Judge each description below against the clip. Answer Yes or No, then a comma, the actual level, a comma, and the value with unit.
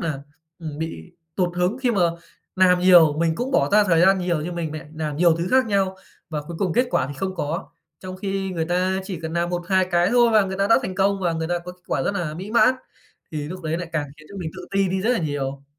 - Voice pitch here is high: No, medium, 180 Hz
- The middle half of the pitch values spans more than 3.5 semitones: No, average, 3.0 semitones